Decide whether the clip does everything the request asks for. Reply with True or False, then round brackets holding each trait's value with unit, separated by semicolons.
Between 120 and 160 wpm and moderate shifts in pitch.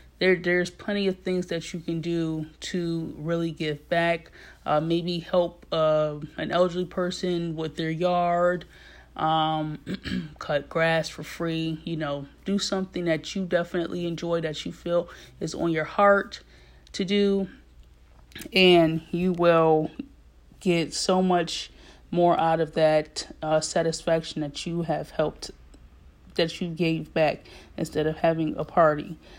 False (145 wpm; 2.2 semitones)